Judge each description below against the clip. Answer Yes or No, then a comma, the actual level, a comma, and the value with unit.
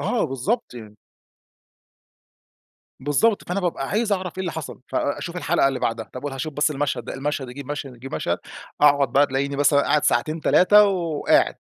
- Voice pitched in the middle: Yes, medium, 145 Hz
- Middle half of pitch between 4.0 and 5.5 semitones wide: Yes, average, 4.5 semitones